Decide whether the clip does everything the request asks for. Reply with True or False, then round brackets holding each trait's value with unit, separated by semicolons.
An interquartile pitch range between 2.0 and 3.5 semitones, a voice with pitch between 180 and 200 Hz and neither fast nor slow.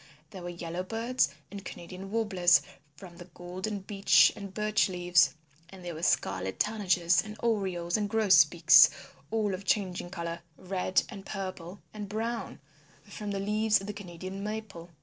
True (3.1 semitones; 190 Hz; 150 wpm)